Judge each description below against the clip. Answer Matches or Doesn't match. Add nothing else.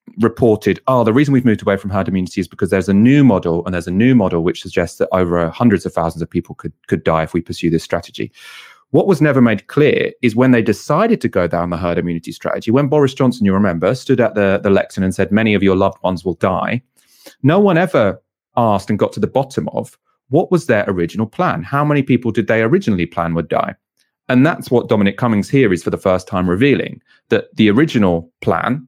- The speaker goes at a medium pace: Doesn't match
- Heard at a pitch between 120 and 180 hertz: Doesn't match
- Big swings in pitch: Matches